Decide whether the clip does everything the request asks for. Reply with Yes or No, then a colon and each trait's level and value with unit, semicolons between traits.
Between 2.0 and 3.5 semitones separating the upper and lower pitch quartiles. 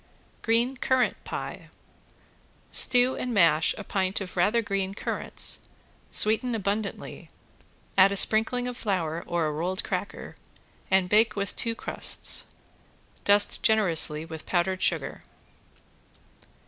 No: average, 3.9 semitones